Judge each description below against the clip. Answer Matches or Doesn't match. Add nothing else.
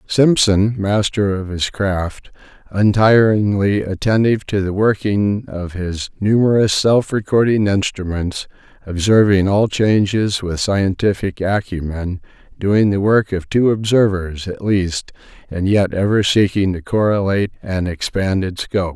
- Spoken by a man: Matches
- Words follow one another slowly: Matches